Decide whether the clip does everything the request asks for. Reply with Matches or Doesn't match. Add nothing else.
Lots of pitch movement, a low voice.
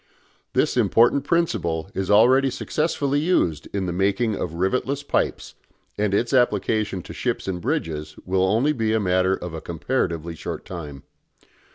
Matches